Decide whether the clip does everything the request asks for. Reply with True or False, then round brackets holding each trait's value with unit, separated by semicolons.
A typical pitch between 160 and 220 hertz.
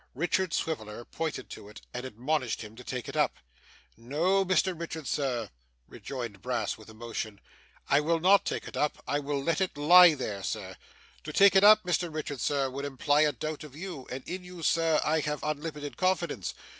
False (150 Hz)